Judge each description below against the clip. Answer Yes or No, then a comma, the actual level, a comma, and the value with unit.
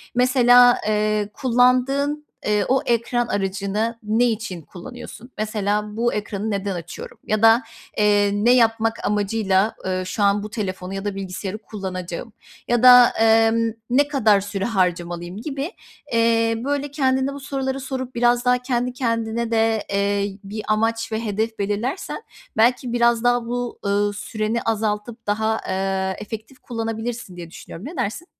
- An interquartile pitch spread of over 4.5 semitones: No, average, 3.1 semitones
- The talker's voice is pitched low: No, high, 225 Hz